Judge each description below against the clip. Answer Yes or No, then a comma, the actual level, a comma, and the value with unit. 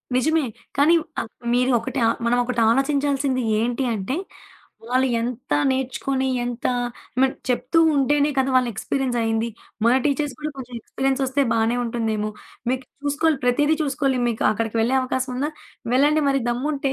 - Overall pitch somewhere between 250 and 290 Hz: Yes, very high, 260 Hz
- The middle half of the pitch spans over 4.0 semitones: No, average, 2.7 semitones